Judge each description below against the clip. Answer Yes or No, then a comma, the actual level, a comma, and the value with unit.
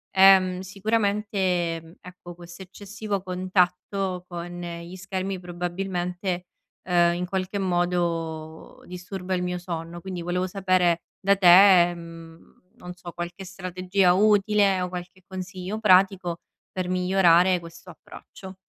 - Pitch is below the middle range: No, medium, 180 Hz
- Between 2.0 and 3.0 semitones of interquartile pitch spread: No, narrow, 1.6 semitones